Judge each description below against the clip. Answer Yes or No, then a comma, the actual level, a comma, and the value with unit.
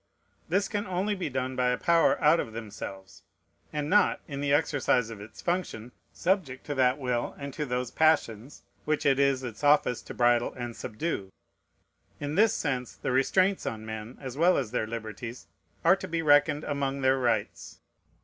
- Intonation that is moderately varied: Yes, average, 4.4 semitones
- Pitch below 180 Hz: Yes, low, 135 Hz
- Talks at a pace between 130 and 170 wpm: No, average, 180 wpm